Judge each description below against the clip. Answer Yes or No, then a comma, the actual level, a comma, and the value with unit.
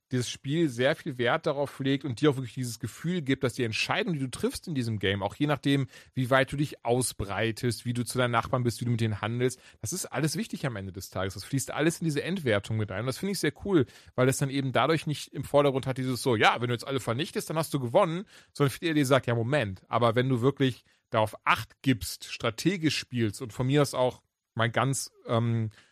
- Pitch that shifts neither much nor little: Yes, average, 4.0 semitones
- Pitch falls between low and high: No, low, 130 Hz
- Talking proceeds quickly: Yes, fast, 250 wpm